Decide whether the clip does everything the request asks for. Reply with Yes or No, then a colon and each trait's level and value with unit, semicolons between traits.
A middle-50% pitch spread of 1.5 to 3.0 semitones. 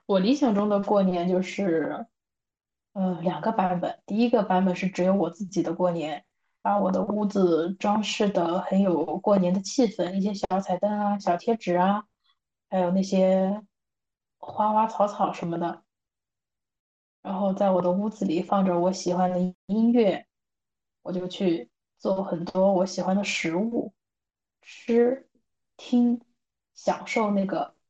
Yes: narrow, 2.4 semitones